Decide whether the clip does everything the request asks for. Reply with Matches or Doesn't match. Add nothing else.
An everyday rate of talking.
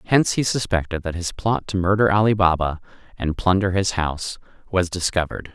Matches